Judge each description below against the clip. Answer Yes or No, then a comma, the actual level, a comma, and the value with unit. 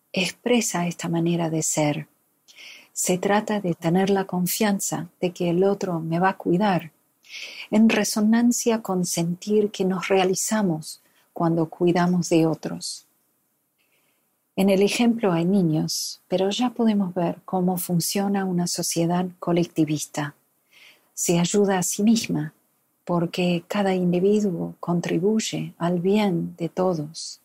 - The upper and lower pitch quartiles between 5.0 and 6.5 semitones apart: No, average, 2.8 semitones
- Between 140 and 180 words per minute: No, slow, 125 wpm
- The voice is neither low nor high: Yes, medium, 180 Hz